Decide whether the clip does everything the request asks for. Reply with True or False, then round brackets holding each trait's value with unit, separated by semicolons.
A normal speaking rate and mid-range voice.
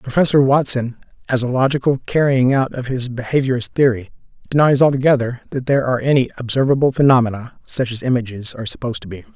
False (165 wpm; 130 Hz)